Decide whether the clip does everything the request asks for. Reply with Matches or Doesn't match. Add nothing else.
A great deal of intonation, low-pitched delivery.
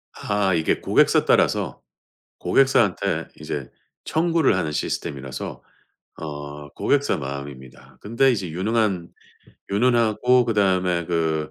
Matches